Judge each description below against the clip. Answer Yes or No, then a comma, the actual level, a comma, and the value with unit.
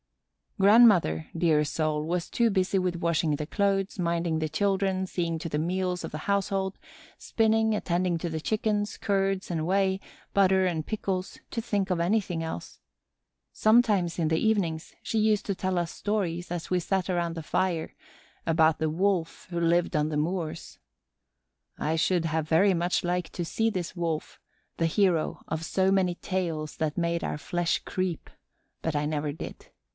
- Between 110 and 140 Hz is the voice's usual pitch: No, medium, 175 Hz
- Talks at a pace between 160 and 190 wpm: Yes, average, 170 wpm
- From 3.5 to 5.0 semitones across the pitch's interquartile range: No, average, 3.1 semitones